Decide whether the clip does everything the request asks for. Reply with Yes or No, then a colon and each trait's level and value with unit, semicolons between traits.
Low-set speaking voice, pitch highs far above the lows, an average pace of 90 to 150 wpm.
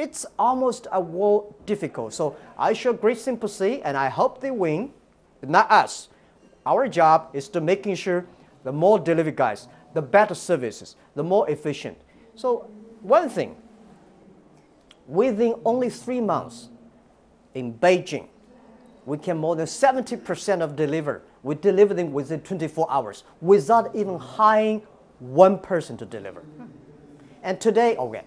No: high, 190 Hz; wide, 6.2 semitones; average, 140 wpm